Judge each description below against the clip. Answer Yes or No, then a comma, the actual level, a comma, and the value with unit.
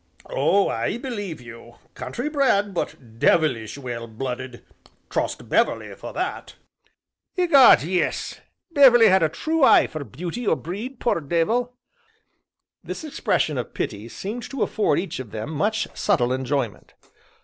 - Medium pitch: Yes, medium, 170 Hz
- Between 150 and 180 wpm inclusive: No, average, 140 wpm